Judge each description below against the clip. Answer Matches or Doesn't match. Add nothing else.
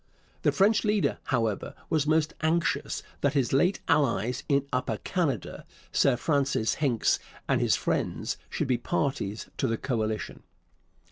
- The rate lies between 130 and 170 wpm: Matches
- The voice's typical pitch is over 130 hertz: Matches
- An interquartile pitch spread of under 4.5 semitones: Doesn't match